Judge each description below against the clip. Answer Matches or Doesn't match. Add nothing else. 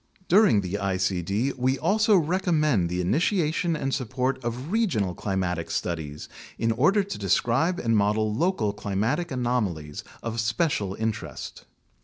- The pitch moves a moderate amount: Doesn't match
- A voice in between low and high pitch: Doesn't match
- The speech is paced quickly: Doesn't match